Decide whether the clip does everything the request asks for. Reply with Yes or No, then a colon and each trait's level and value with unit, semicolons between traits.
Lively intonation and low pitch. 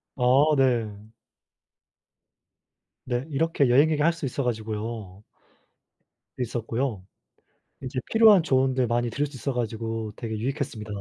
No: average, 3.6 semitones; low, 125 Hz